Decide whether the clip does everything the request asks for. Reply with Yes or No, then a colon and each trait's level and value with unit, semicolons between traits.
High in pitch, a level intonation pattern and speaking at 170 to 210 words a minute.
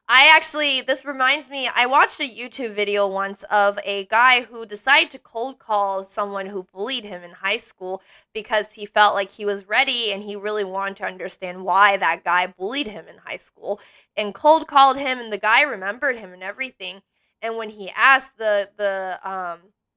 No: high, 210 Hz; average, 4.6 semitones; average, 195 wpm